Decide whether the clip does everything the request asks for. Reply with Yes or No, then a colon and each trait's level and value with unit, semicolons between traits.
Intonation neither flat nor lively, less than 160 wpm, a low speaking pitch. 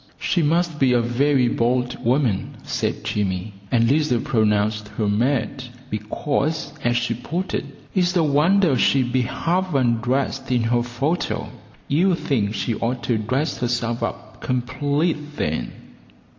Yes: average, 4.3 semitones; average, 140 wpm; low, 125 Hz